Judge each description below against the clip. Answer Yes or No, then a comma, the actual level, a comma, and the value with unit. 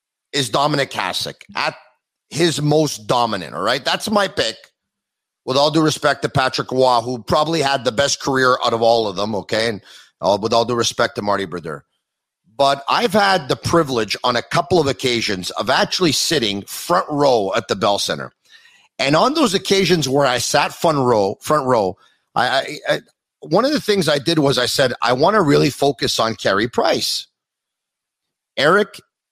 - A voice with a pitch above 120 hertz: Yes, medium, 140 Hz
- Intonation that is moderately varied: No, wide, 5.8 semitones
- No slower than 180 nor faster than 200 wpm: Yes, average, 185 wpm